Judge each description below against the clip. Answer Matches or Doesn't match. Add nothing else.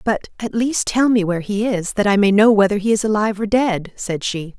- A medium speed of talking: Doesn't match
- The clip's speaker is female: Matches